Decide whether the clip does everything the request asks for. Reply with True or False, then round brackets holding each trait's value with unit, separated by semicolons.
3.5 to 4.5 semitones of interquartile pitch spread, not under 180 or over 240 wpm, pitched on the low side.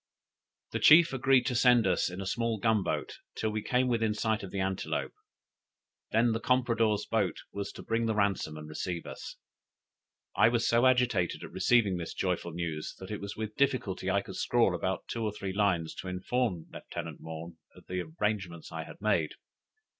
True (4.2 semitones; 190 wpm; 105 Hz)